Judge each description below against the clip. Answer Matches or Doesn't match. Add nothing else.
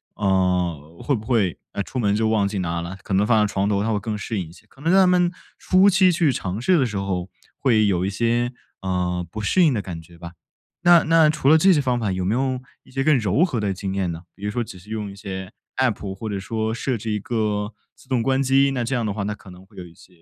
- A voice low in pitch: Matches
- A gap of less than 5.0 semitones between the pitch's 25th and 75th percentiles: Doesn't match